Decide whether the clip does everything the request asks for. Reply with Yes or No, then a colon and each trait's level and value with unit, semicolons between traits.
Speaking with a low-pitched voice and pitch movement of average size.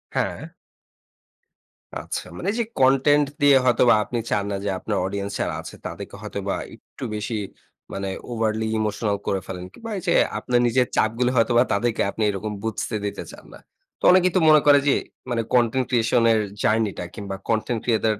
Yes: low, 115 Hz; average, 3.2 semitones